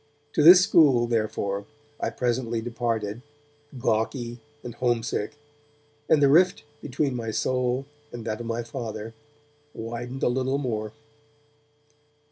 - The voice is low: Yes, low, 120 Hz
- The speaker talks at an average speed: No, slow, 120 wpm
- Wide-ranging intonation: No, narrow, 2.5 semitones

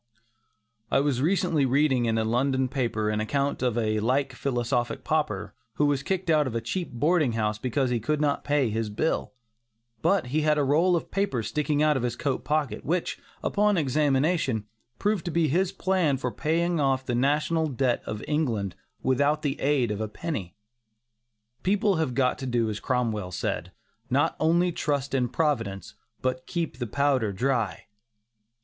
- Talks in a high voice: No, low, 135 Hz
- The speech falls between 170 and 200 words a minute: Yes, average, 175 wpm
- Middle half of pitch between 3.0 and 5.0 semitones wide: Yes, average, 4.3 semitones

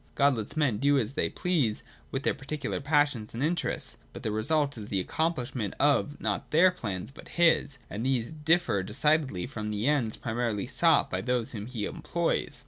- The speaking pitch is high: No, low, 130 Hz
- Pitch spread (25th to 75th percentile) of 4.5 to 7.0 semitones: Yes, wide, 5.6 semitones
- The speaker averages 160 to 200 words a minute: Yes, average, 180 wpm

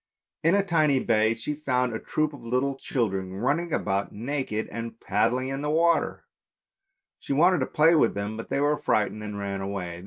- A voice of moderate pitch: No, low, 125 Hz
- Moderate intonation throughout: No, wide, 5.8 semitones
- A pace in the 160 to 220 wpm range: Yes, average, 190 wpm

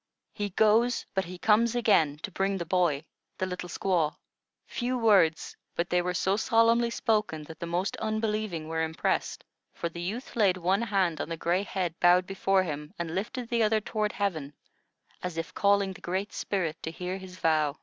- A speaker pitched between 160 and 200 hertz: Yes, medium, 185 Hz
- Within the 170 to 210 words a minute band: Yes, average, 190 wpm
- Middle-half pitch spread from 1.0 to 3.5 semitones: No, average, 3.9 semitones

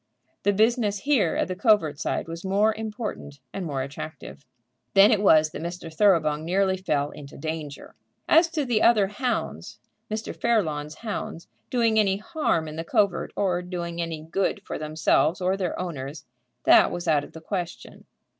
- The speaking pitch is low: No, medium, 180 Hz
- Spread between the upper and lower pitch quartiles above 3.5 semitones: Yes, average, 5.2 semitones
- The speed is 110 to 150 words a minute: No, average, 170 wpm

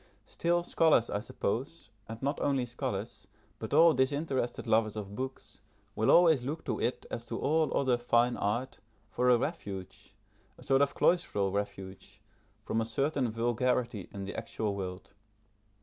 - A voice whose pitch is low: Yes, low, 120 Hz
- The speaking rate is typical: Yes, average, 155 wpm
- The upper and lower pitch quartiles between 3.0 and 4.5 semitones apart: No, average, 5.1 semitones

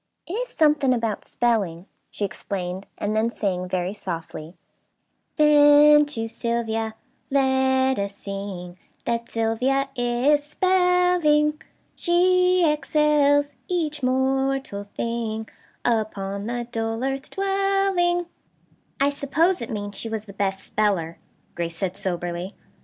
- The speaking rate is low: Yes, slow, 115 wpm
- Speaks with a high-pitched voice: Yes, high, 240 Hz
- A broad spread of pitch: Yes, wide, 6.7 semitones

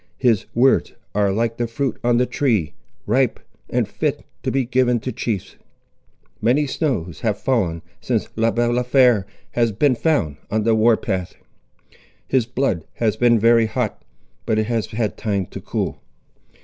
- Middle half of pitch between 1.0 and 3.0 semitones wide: Yes, average, 2.7 semitones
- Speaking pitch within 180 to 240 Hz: No, low, 115 Hz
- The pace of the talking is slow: No, average, 160 wpm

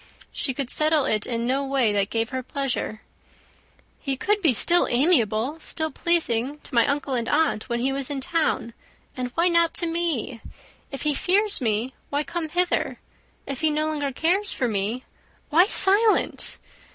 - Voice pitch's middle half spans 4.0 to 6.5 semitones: Yes, average, 5.3 semitones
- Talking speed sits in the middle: Yes, average, 175 wpm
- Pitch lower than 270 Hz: No, very high, 275 Hz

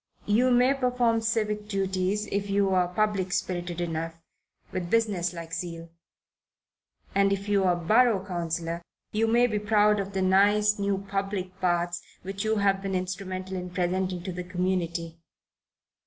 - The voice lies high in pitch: Yes, high, 195 Hz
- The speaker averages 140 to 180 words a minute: Yes, average, 155 wpm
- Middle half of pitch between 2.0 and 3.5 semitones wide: Yes, average, 2.7 semitones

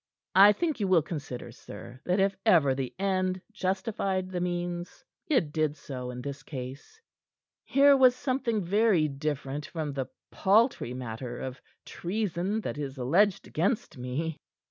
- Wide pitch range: Yes, wide, 6.4 semitones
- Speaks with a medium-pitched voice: Yes, medium, 175 Hz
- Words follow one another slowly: No, average, 145 wpm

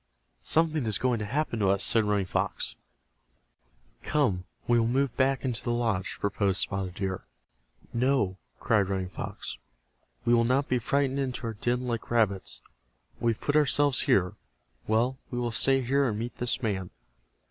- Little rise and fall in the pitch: No, average, 4.5 semitones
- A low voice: Yes, low, 120 Hz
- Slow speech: No, average, 170 wpm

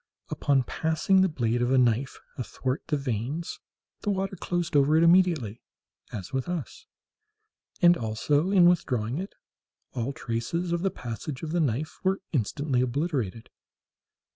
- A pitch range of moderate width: No, wide, 6.0 semitones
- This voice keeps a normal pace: Yes, average, 145 wpm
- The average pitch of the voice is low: No, medium, 145 Hz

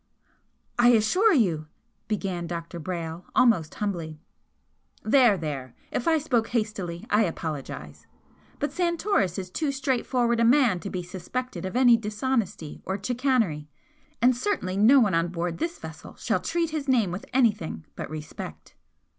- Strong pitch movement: Yes, wide, 6.8 semitones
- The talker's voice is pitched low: No, high, 210 Hz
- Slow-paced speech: No, average, 150 wpm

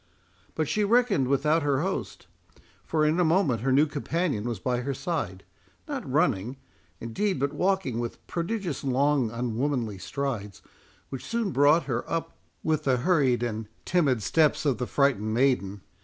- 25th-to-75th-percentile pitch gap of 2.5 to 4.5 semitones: No, average, 5.3 semitones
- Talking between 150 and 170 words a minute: Yes, average, 155 wpm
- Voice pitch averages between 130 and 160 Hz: Yes, medium, 140 Hz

